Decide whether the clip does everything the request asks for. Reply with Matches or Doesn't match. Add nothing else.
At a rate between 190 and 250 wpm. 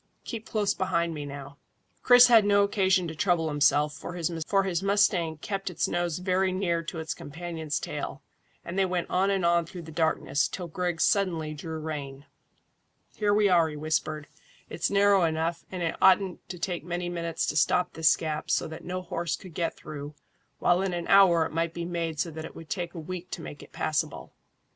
Matches